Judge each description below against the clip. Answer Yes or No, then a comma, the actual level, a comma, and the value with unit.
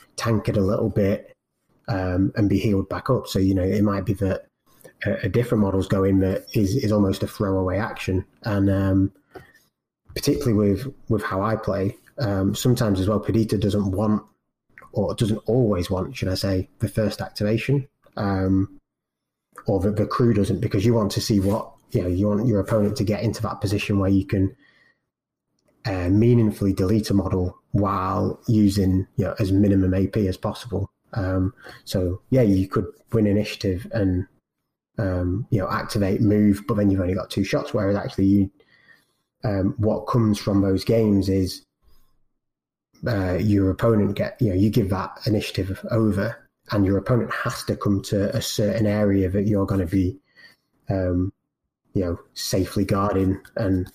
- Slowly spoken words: No, average, 175 wpm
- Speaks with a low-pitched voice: Yes, low, 100 Hz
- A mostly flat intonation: Yes, narrow, 2.1 semitones